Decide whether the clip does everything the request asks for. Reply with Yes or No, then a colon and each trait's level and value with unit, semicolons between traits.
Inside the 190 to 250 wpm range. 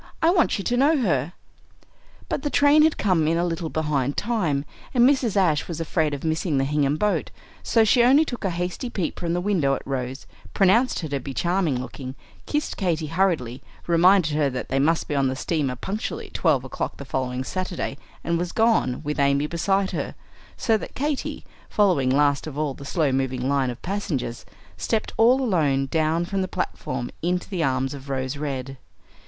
Yes: average, 195 wpm